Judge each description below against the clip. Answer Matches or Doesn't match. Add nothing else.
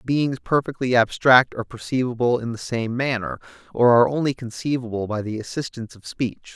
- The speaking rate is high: Doesn't match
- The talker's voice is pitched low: Matches